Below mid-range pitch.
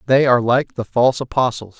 Yes: low, 125 Hz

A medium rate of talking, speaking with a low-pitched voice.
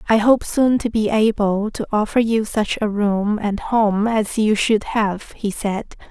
No: average, 195 wpm; high, 215 Hz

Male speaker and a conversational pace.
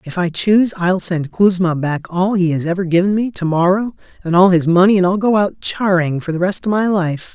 No: male; fast, 245 wpm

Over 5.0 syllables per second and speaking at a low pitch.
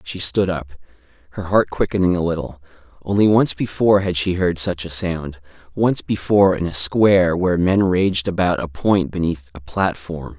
No: 4.9 syllables/s; very low, 90 Hz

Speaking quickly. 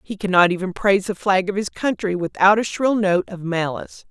Yes: fast, 220 wpm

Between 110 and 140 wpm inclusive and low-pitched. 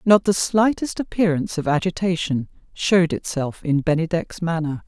No: slow, 135 wpm; medium, 170 Hz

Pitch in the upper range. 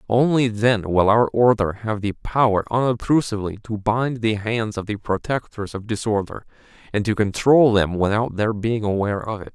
No: low, 110 Hz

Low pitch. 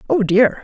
No: high, 220 Hz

